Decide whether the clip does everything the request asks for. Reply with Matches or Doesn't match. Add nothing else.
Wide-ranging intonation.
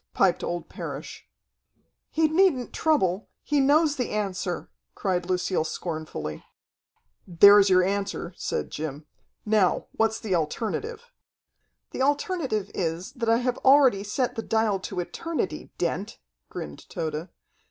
Matches